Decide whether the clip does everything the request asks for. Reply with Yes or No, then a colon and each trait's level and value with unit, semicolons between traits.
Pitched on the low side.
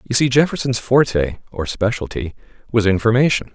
Yes: low, 115 Hz